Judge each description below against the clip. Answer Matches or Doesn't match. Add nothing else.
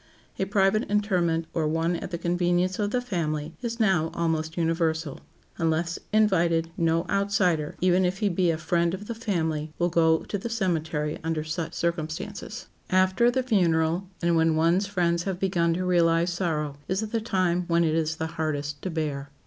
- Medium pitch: Matches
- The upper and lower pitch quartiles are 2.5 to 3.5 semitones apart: Matches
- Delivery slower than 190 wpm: Matches